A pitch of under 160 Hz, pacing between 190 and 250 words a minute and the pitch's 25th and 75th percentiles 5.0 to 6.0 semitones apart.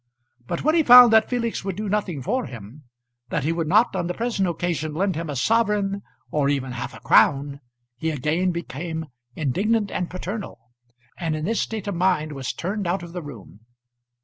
No: medium, 175 Hz; average, 195 wpm; wide, 5.4 semitones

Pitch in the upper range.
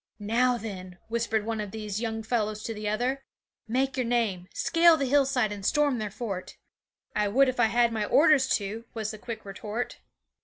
Yes: high, 225 Hz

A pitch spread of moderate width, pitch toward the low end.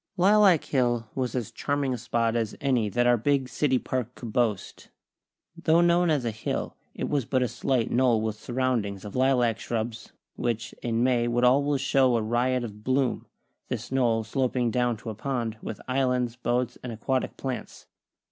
No: narrow, 2.3 semitones; low, 125 Hz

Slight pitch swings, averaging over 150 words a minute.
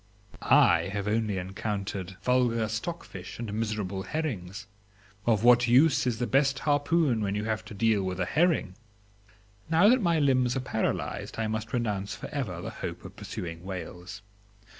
No: average, 4.7 semitones; average, 160 wpm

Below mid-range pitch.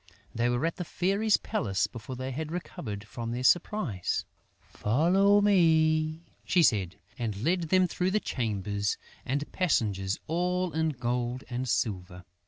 Yes: low, 130 Hz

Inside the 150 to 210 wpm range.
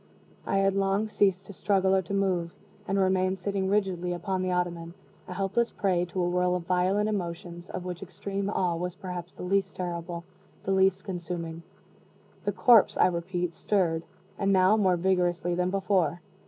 Yes: average, 175 wpm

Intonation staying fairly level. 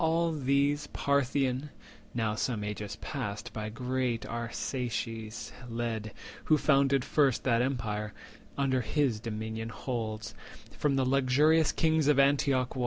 No: average, 3.8 semitones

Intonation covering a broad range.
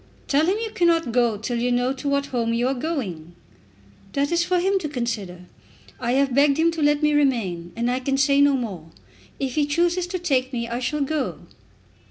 No: average, 4.2 semitones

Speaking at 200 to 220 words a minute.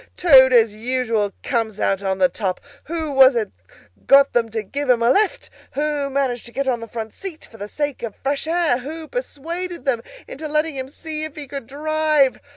Yes: fast, 205 wpm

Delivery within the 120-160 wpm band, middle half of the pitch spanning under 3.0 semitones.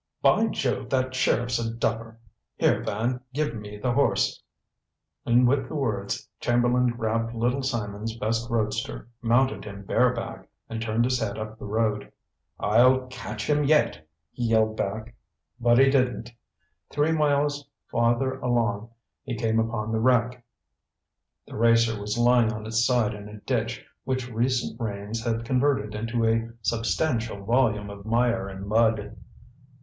Yes: average, 150 wpm; narrow, 2.4 semitones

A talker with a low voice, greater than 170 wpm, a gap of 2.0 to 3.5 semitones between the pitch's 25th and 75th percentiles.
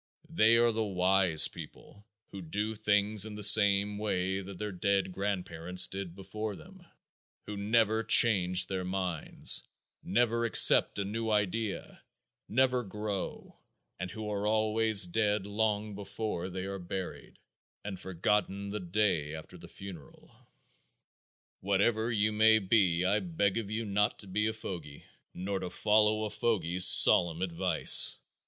No: low, 100 Hz; average, 145 wpm; narrow, 2.6 semitones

